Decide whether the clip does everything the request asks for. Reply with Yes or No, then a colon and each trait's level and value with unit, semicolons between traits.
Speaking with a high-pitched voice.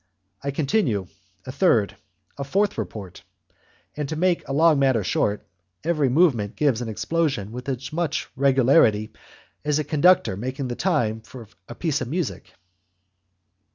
No: low, 135 Hz